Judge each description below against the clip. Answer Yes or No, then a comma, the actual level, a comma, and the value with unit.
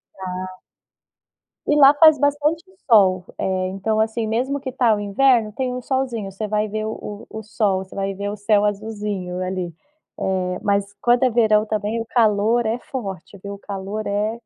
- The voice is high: Yes, high, 215 Hz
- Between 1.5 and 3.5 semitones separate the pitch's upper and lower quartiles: Yes, average, 3.2 semitones